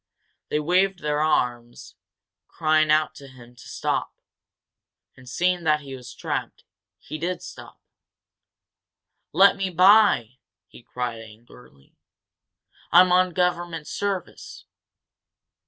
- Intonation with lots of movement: Yes, wide, 6.3 semitones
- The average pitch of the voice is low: No, medium, 155 Hz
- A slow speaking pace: Yes, slow, 110 wpm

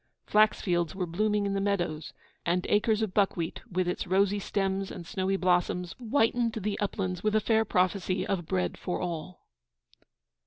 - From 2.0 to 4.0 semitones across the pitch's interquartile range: Yes, narrow, 2.6 semitones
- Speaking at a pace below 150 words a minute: No, average, 165 wpm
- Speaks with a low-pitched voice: No, high, 190 Hz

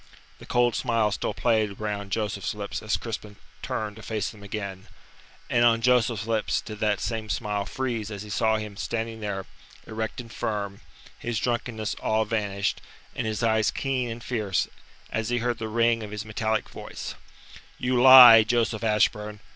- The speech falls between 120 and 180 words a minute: Yes, average, 170 wpm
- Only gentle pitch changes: Yes, narrow, 1.7 semitones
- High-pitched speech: No, low, 110 Hz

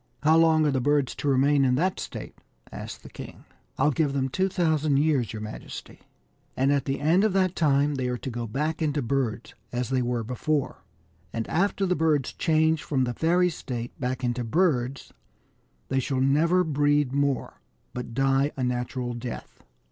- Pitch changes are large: No, average, 3.8 semitones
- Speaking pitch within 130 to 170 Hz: Yes, medium, 140 Hz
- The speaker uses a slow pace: No, average, 190 wpm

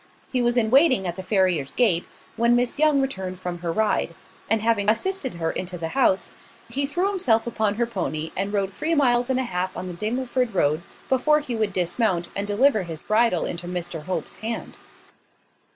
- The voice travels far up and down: Yes, wide, 5.7 semitones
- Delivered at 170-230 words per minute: Yes, average, 195 wpm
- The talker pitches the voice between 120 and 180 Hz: No, high, 215 Hz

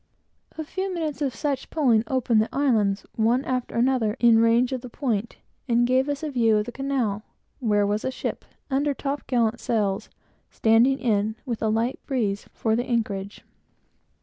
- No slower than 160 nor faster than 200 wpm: Yes, average, 175 wpm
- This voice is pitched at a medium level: No, high, 240 Hz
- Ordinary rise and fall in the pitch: Yes, average, 3.4 semitones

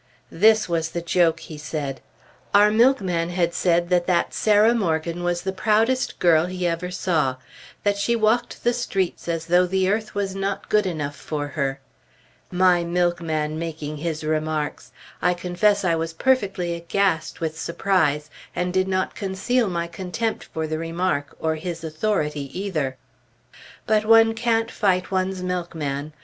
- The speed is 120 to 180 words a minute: Yes, average, 155 wpm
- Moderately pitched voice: Yes, medium, 175 Hz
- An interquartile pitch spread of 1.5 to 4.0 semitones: Yes, average, 3.6 semitones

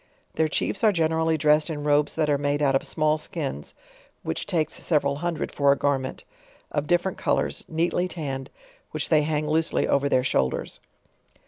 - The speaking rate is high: No, average, 175 wpm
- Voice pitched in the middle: Yes, medium, 150 Hz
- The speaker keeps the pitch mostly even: Yes, narrow, 2.3 semitones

